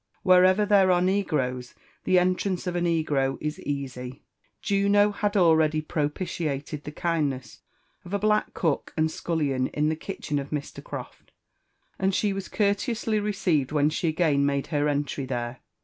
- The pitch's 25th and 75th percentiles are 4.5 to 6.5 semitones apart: Yes, average, 4.9 semitones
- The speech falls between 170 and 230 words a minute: No, average, 160 wpm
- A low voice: No, medium, 160 Hz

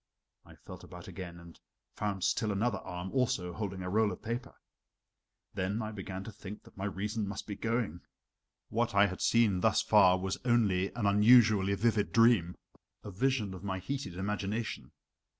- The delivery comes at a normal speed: Yes, average, 170 wpm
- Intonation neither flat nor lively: Yes, average, 3.1 semitones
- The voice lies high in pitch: No, low, 100 Hz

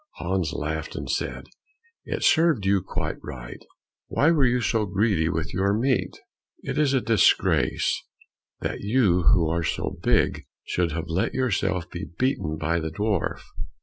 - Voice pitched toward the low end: Yes, very low, 95 Hz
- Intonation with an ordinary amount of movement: No, wide, 6.7 semitones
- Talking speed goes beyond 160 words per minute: No, average, 155 wpm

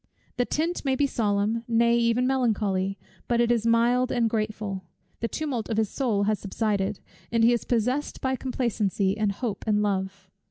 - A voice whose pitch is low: No, high, 230 Hz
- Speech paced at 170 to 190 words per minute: Yes, average, 175 wpm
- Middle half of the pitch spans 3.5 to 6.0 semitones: No, average, 3.0 semitones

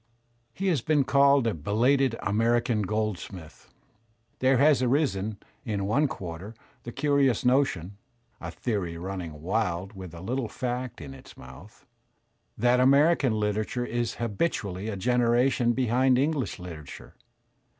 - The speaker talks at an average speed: No, slow, 130 wpm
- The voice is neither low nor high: No, low, 115 Hz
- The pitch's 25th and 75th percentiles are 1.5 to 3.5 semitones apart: No, average, 5.1 semitones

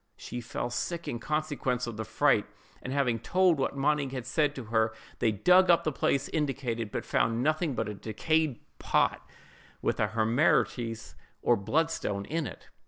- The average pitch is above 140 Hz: No, low, 130 Hz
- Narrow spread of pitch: No, average, 5.2 semitones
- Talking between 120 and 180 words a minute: Yes, average, 170 wpm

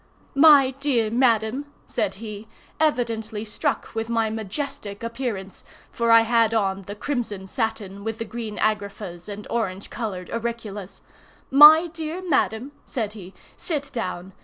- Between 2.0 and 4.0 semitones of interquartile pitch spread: Yes, average, 3.1 semitones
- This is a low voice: No, high, 225 Hz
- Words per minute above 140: No, slow, 135 wpm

